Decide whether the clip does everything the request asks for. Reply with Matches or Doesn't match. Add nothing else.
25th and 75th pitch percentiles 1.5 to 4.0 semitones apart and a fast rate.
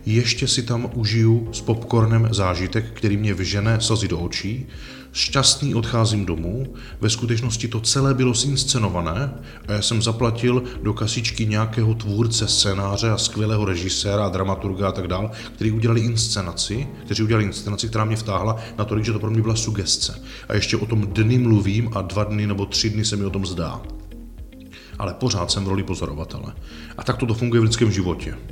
Matches